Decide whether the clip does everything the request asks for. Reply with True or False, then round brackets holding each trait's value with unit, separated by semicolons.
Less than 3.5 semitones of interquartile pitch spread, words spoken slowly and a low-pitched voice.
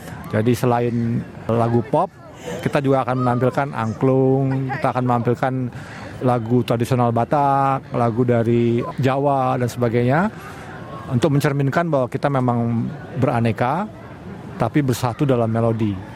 False (2.4 semitones; 110 wpm; 125 Hz)